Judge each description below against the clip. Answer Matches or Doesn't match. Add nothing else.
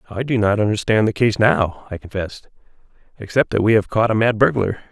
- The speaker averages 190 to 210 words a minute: Matches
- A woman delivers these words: Doesn't match